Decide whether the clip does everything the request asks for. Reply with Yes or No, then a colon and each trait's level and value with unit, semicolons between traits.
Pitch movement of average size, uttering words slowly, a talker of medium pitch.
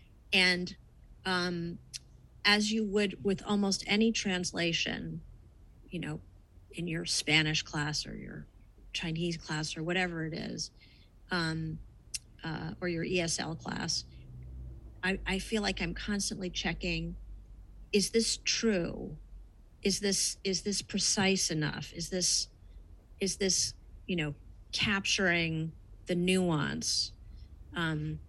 Yes: average, 4.4 semitones; slow, 115 wpm; medium, 170 Hz